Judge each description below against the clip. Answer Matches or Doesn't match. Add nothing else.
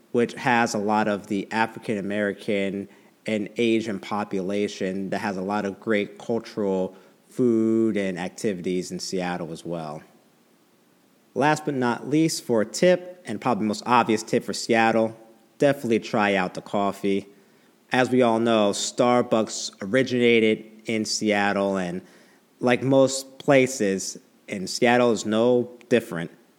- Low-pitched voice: Matches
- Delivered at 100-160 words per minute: Matches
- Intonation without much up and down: Doesn't match